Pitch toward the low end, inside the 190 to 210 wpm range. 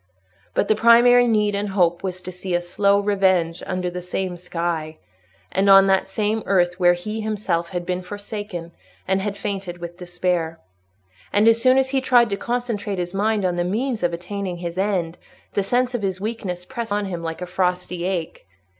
No: high, 190 Hz; average, 195 wpm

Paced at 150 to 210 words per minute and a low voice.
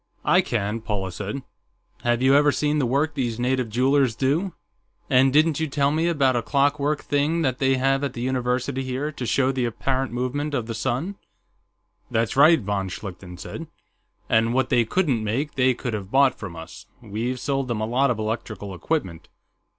Yes: average, 185 wpm; low, 130 Hz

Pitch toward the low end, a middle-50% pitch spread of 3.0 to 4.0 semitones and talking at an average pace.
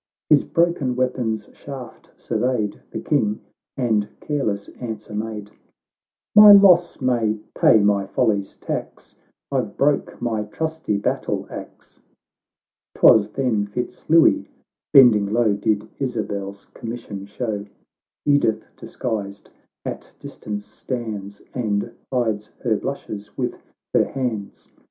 No: low, 110 Hz; average, 3.7 semitones; slow, 115 wpm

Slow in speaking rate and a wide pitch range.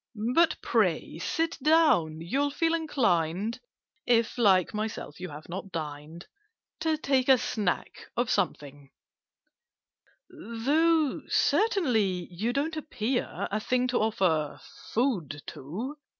Yes: slow, 115 wpm; wide, 8.4 semitones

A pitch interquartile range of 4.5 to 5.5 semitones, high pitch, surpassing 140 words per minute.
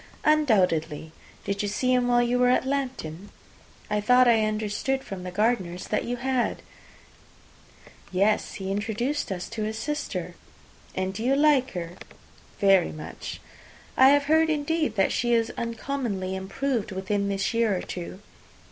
Yes: average, 4.9 semitones; high, 220 Hz; average, 155 wpm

